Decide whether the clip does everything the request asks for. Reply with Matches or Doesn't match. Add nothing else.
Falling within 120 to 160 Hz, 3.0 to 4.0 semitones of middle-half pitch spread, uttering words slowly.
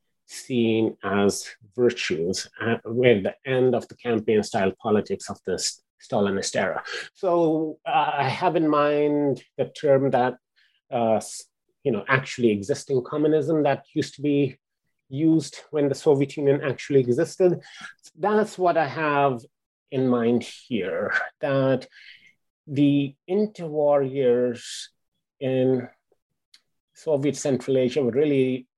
Matches